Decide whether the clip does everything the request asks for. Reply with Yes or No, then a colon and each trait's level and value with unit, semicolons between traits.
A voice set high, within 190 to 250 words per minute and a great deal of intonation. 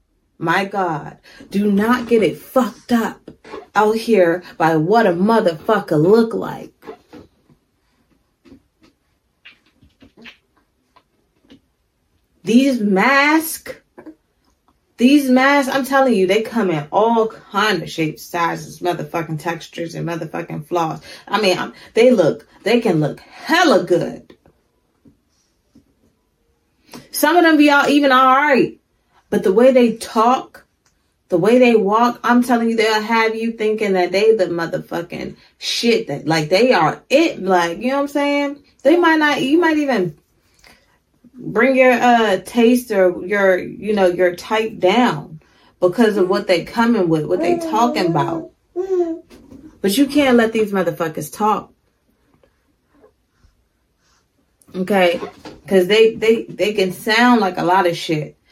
No: high, 220 Hz; slow, 135 wpm; wide, 6.1 semitones